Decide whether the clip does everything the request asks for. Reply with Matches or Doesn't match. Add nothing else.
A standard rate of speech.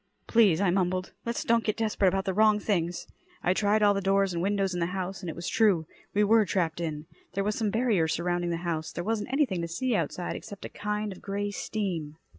Doesn't match